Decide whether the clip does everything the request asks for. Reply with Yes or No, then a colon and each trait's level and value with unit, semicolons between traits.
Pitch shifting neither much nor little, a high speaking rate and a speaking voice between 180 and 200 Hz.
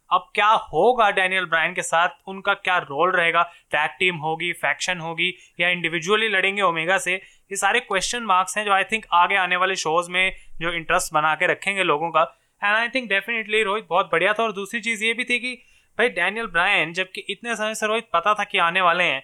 Yes: average, 3.5 semitones; fast, 220 wpm; medium, 185 Hz